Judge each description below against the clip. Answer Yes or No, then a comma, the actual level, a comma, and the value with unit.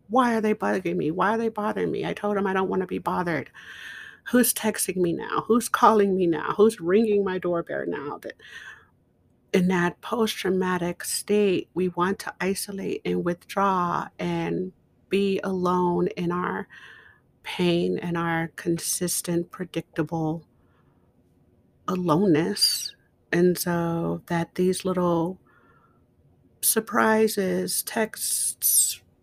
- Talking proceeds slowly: Yes, slow, 125 wpm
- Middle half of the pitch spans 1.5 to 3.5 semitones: Yes, average, 2.8 semitones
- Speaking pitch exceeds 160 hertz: Yes, medium, 185 Hz